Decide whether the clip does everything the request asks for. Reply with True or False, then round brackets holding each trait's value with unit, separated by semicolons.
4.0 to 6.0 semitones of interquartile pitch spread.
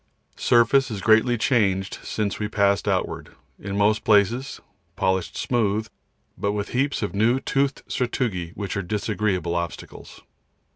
False (3.1 semitones)